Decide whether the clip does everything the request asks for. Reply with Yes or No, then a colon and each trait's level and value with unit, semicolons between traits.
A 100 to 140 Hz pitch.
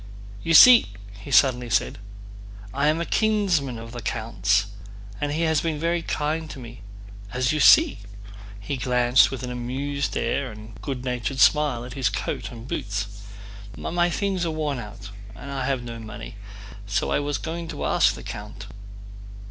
Yes: low, 135 Hz